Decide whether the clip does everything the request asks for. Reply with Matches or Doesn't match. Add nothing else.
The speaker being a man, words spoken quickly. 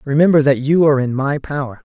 Matches